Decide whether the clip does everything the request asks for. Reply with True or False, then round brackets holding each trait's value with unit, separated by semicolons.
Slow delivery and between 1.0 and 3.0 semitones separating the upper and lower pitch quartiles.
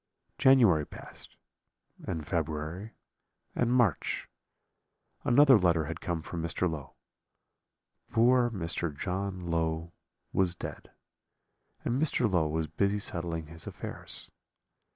False (110 wpm; 4.7 semitones)